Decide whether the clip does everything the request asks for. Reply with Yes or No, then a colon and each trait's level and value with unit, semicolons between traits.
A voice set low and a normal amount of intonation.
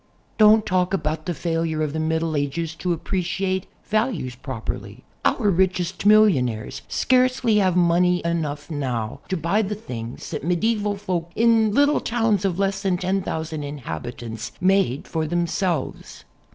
No: medium, 175 Hz; average, 4.5 semitones